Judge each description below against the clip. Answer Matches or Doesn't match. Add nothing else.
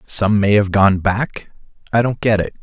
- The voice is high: Doesn't match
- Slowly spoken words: Doesn't match